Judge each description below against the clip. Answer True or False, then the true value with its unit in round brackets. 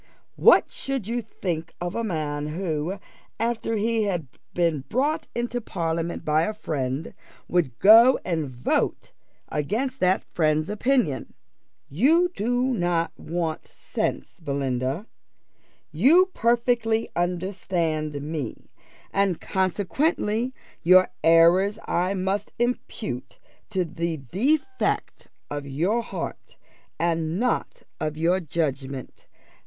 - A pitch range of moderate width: False (6.4 semitones)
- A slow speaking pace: True (110 wpm)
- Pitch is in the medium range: True (180 Hz)